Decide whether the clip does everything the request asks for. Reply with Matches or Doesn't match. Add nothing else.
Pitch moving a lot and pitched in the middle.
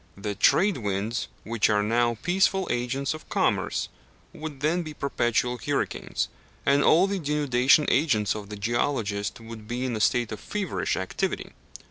Doesn't match